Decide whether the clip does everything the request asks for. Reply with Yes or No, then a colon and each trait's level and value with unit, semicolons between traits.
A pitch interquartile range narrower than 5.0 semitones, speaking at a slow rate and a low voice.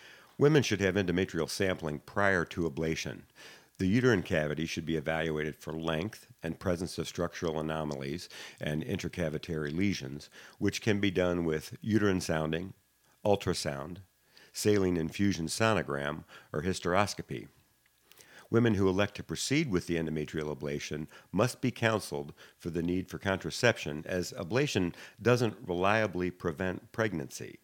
Yes: average, 4.1 semitones; slow, 130 wpm; very low, 90 Hz